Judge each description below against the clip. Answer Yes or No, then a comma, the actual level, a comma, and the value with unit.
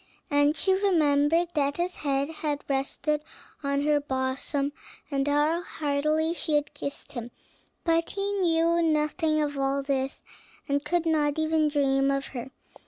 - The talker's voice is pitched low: No, very high, 295 Hz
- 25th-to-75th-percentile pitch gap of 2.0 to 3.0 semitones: Yes, narrow, 2.5 semitones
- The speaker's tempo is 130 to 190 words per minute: Yes, average, 150 wpm